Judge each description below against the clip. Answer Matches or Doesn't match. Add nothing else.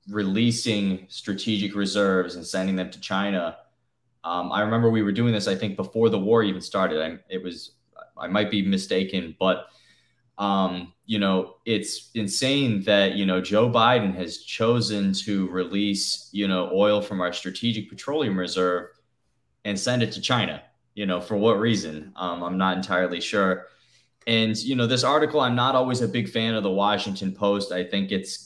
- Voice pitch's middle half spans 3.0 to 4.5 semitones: Matches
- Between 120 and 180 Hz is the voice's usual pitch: Doesn't match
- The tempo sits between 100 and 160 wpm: Doesn't match